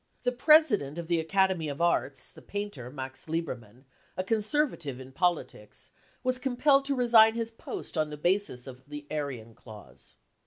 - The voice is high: No, medium, 170 Hz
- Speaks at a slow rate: No, average, 160 wpm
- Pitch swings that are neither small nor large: No, wide, 8.7 semitones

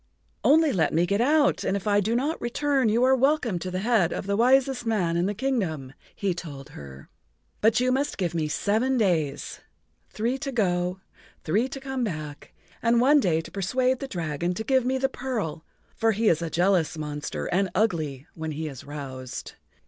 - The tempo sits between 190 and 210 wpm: Yes, average, 195 wpm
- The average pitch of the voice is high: Yes, high, 200 Hz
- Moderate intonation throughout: No, wide, 7.7 semitones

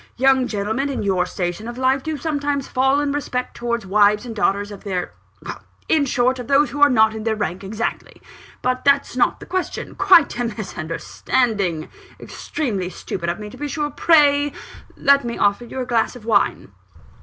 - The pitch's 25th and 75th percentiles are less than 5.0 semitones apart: No, average, 5.3 semitones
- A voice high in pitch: Yes, high, 245 Hz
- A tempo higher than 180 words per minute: Yes, average, 190 wpm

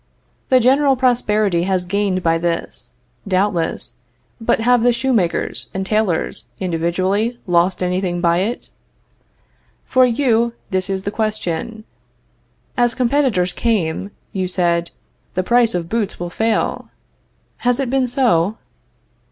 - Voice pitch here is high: Yes, high, 205 Hz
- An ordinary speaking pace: No, slow, 125 wpm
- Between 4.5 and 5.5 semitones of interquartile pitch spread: Yes, average, 5.0 semitones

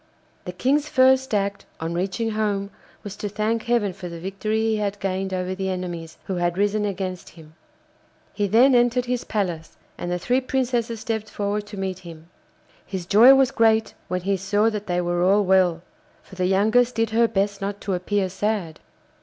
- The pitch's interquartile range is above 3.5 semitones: No, average, 3.2 semitones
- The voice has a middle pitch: No, high, 200 Hz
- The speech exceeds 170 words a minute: Yes, average, 190 wpm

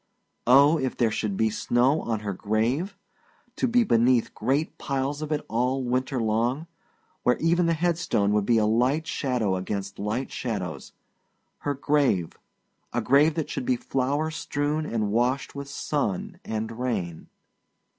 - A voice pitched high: No, low, 130 Hz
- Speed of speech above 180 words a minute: No, average, 155 wpm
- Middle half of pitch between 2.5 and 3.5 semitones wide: No, average, 5.0 semitones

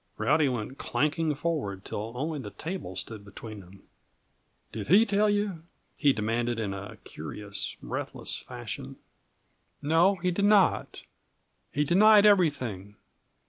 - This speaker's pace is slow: Yes, slow, 125 wpm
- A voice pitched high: No, medium, 145 Hz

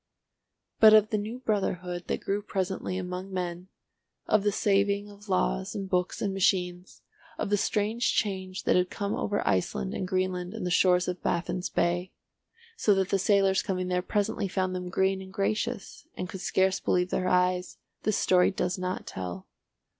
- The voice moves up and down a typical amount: No, narrow, 1.8 semitones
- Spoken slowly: No, average, 175 wpm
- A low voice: No, medium, 185 Hz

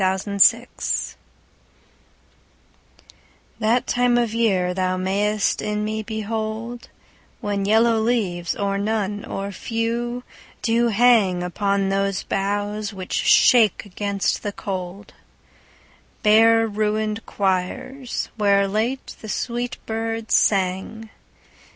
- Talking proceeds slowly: Yes, slow, 100 wpm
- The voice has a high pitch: Yes, high, 210 Hz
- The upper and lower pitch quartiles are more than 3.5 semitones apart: No, narrow, 2.4 semitones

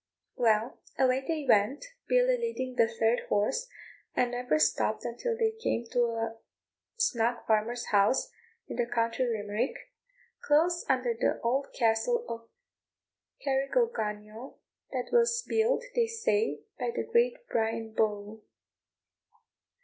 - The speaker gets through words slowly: Yes, slow, 125 wpm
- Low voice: No, high, 245 Hz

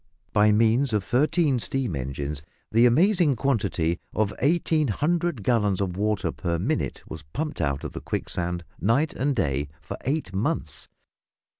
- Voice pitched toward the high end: No, low, 110 Hz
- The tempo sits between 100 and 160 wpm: Yes, average, 145 wpm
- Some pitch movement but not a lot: No, wide, 8.1 semitones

